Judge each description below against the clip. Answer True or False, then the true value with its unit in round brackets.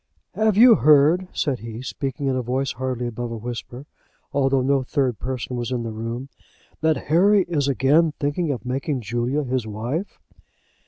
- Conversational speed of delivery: True (170 wpm)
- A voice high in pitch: False (130 Hz)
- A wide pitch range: False (3.5 semitones)